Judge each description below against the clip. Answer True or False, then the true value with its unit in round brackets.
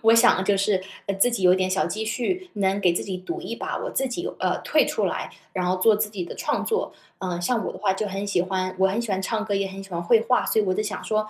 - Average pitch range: True (3.0 semitones)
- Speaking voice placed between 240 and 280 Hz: False (200 Hz)